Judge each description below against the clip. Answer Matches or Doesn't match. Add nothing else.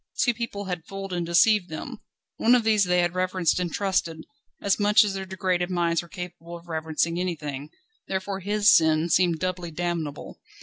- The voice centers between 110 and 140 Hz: Doesn't match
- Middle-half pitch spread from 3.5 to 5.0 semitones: Doesn't match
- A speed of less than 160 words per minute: Doesn't match